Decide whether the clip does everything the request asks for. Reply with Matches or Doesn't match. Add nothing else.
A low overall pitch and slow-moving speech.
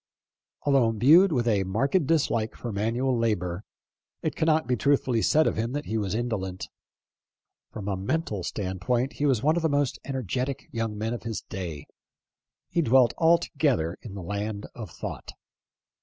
Doesn't match